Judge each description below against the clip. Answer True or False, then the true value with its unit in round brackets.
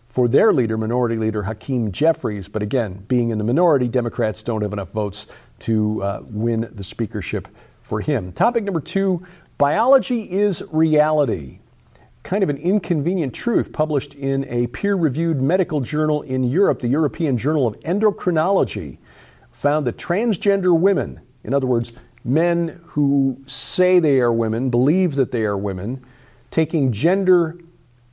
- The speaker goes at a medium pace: True (150 wpm)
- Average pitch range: False (6.3 semitones)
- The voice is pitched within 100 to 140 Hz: True (135 Hz)